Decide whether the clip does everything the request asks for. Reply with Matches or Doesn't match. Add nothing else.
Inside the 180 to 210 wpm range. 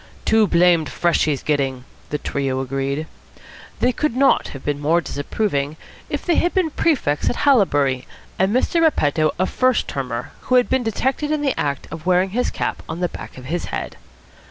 Matches